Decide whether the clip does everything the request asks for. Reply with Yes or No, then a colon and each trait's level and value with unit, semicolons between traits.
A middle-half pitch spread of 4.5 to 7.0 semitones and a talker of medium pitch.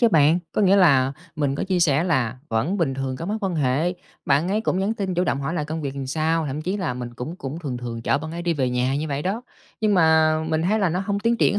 Yes: average, 5.2 semitones; medium, 160 Hz